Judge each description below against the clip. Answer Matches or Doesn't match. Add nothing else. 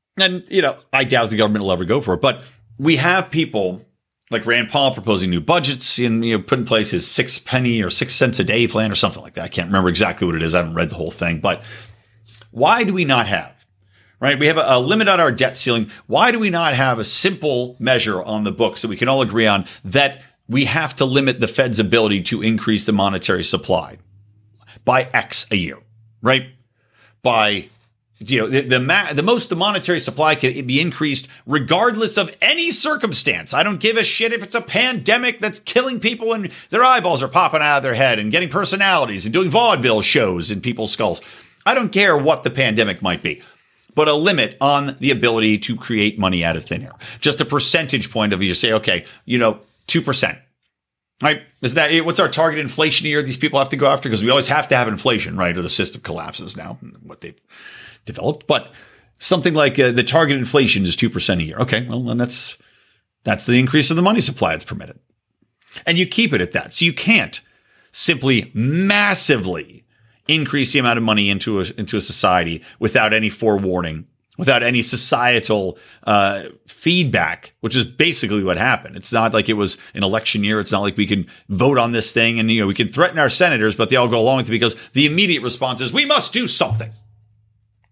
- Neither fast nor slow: Doesn't match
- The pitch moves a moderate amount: Doesn't match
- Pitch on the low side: Matches